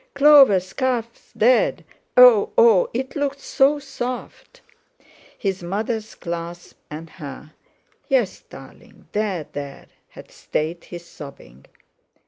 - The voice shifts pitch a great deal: Yes, wide, 7.1 semitones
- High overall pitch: Yes, high, 210 Hz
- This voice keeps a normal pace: No, slow, 110 wpm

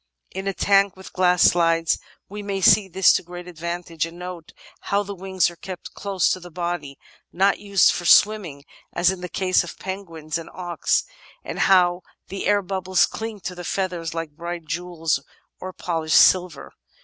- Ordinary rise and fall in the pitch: No, narrow, 2.1 semitones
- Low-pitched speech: No, medium, 180 Hz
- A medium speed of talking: Yes, average, 185 wpm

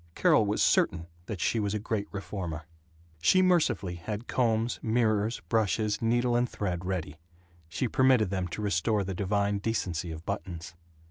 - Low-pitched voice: Yes, low, 105 Hz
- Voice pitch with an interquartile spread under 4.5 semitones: Yes, average, 3.9 semitones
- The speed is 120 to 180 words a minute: Yes, average, 155 wpm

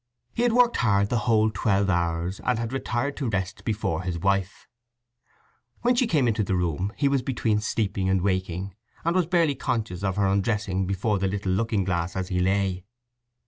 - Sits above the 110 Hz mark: No, low, 100 Hz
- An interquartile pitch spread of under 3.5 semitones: No, average, 4.1 semitones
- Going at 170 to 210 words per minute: Yes, average, 190 wpm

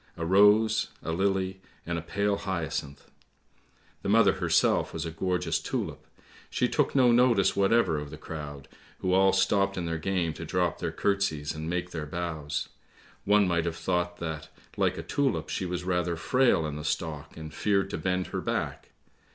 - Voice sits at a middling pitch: No, very low, 90 Hz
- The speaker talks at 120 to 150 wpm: No, average, 180 wpm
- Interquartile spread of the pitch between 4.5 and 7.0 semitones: No, average, 3.3 semitones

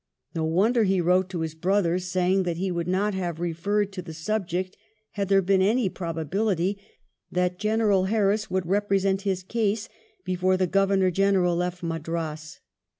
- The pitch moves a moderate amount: No, narrow, 2.2 semitones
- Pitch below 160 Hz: No, medium, 185 Hz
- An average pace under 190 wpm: Yes, average, 165 wpm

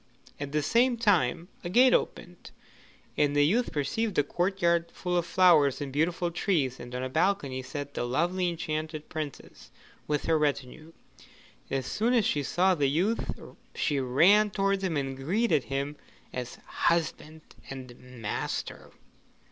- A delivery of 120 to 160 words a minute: Yes, average, 155 wpm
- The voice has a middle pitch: Yes, medium, 155 Hz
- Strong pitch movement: No, average, 5.0 semitones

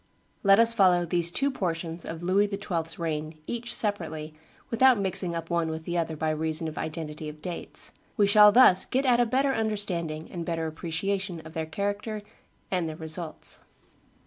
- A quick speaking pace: No, average, 175 wpm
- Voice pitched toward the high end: No, medium, 175 Hz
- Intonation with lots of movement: No, average, 4.2 semitones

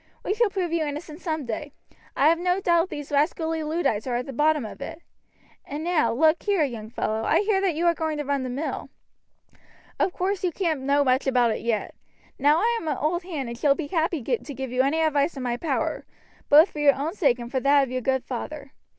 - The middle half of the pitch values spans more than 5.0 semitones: No, average, 4.2 semitones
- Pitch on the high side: Yes, very high, 295 Hz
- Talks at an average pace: No, fast, 235 wpm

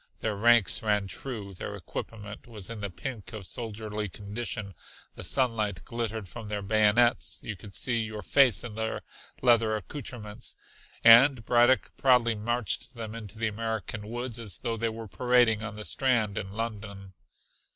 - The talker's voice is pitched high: No, low, 110 Hz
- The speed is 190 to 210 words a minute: No, average, 160 wpm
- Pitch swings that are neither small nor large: No, narrow, 2.3 semitones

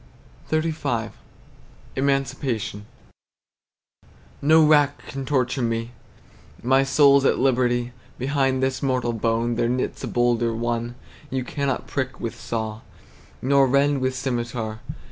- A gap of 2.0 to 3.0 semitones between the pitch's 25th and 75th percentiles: Yes, average, 2.7 semitones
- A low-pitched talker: Yes, low, 130 Hz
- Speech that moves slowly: Yes, slow, 115 wpm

